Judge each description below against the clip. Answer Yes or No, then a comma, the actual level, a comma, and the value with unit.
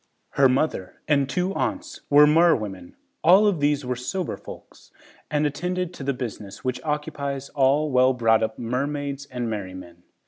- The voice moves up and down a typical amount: Yes, average, 3.7 semitones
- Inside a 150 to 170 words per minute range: Yes, average, 160 wpm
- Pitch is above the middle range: No, medium, 140 Hz